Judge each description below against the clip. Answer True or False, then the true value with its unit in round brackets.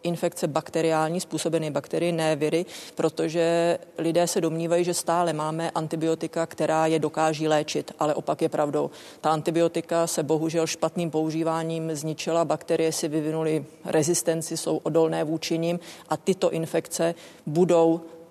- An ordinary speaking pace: True (135 wpm)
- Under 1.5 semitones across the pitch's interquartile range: True (1.0 semitones)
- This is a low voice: False (165 Hz)